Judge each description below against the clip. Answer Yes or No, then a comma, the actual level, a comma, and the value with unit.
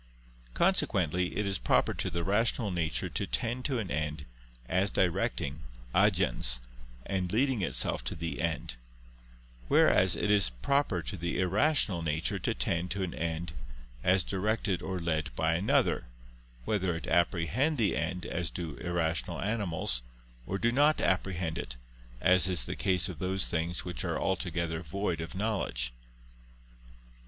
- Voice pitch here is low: Yes, very low, 90 Hz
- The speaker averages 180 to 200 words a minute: No, average, 150 wpm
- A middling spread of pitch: Yes, average, 3.4 semitones